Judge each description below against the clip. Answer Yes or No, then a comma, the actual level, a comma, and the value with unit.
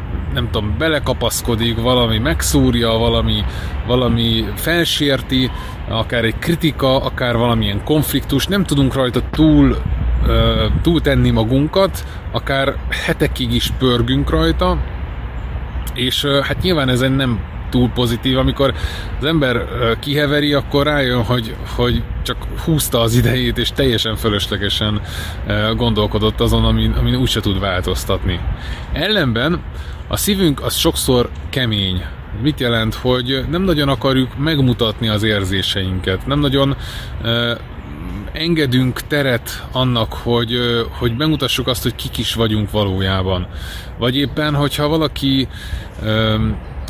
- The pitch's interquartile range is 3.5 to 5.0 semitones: Yes, average, 4.4 semitones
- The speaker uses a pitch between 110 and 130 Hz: Yes, low, 120 Hz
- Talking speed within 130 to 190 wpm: No, average, 120 wpm